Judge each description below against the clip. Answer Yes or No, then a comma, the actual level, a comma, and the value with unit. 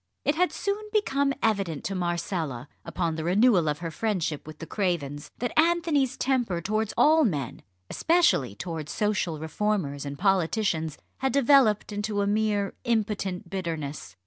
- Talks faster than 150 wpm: No, average, 145 wpm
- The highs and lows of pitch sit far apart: Yes, wide, 6.6 semitones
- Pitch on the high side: Yes, high, 195 Hz